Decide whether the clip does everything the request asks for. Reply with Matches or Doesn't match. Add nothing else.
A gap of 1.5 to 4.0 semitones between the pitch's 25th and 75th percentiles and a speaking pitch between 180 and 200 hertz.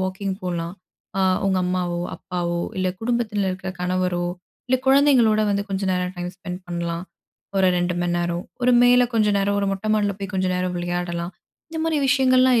Matches